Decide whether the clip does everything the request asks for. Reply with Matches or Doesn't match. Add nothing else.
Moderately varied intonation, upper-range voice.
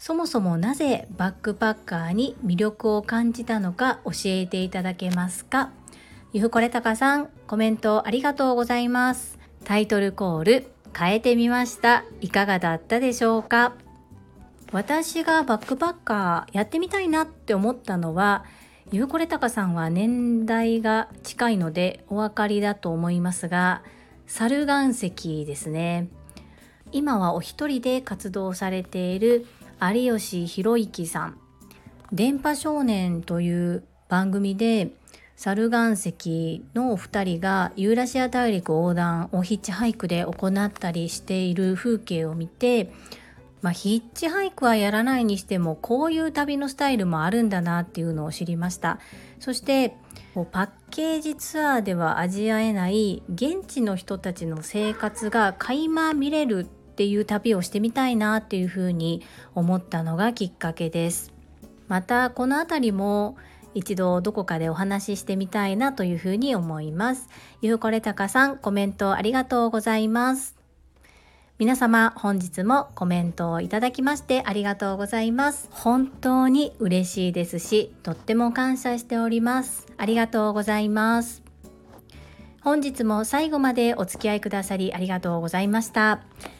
Matches